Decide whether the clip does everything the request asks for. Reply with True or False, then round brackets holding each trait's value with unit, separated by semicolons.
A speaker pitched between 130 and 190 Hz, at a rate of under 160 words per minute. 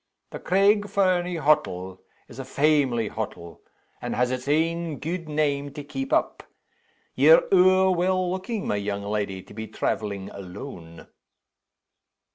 True (140 Hz; 135 wpm)